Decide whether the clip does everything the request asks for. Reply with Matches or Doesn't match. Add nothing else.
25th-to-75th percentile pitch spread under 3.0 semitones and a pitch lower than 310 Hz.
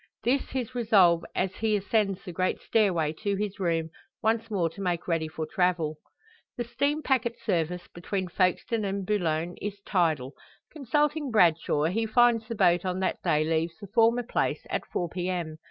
Doesn't match